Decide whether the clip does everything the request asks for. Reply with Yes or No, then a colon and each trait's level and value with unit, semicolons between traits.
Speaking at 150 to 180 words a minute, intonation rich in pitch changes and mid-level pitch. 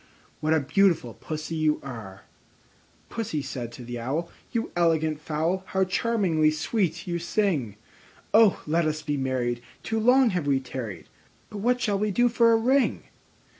Yes: average, 170 wpm; wide, 7.1 semitones; medium, 160 Hz